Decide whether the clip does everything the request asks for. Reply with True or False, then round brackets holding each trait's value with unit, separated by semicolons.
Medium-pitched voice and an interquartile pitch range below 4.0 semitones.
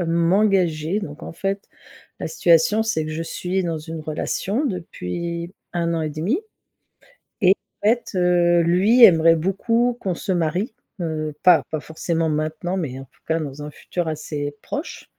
True (170 Hz; 3.5 semitones)